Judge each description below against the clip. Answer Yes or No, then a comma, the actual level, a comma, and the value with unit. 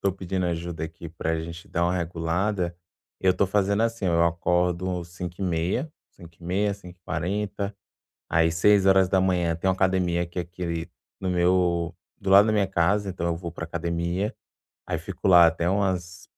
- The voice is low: Yes, very low, 90 Hz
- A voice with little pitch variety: Yes, narrow, 2.1 semitones